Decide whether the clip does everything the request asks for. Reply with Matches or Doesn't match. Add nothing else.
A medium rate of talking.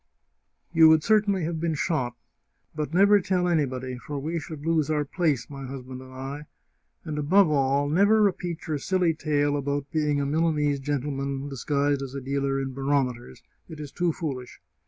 Matches